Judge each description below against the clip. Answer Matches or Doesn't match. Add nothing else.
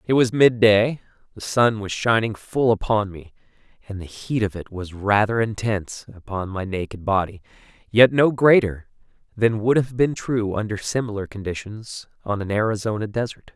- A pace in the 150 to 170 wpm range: Matches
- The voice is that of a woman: Doesn't match